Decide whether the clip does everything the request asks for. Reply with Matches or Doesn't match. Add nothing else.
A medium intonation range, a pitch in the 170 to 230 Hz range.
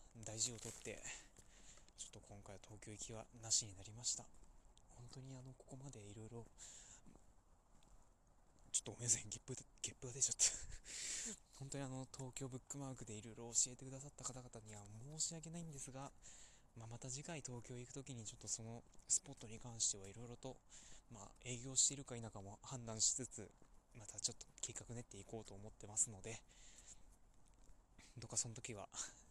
Doesn't match